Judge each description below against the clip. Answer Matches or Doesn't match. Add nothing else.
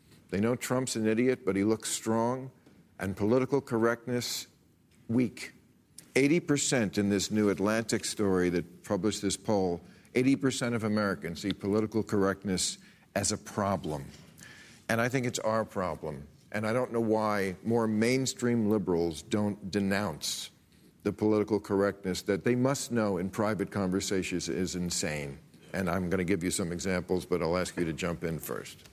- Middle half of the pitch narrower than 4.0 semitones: Matches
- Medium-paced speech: Matches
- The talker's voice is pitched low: Matches